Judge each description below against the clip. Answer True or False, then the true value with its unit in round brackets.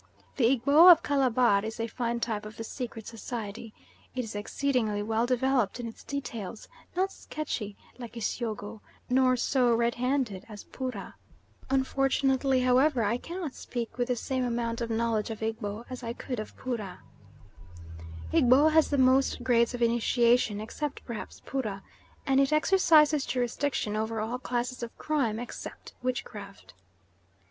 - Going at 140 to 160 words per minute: True (150 wpm)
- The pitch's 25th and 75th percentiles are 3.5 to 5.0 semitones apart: False (3.0 semitones)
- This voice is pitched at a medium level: False (240 Hz)